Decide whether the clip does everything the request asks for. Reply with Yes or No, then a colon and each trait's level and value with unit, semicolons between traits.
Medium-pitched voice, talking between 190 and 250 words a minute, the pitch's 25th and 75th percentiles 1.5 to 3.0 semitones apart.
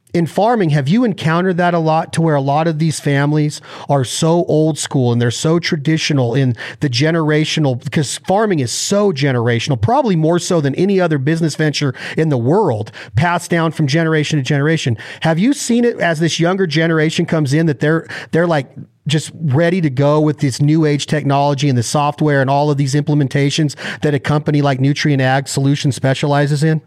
Yes: medium, 150 Hz; average, 195 wpm; narrow, 2.5 semitones